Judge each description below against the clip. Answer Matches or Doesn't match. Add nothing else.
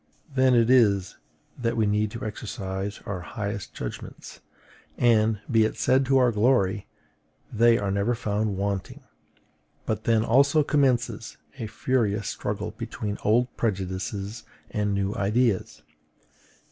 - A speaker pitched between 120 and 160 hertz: Doesn't match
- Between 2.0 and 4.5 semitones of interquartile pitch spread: Matches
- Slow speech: Matches